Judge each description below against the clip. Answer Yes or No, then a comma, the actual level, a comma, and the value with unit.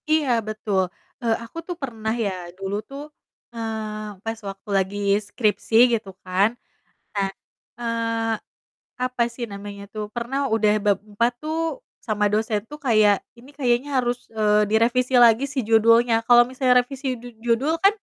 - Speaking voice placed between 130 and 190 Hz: No, high, 225 Hz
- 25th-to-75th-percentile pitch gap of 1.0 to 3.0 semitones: Yes, narrow, 2.6 semitones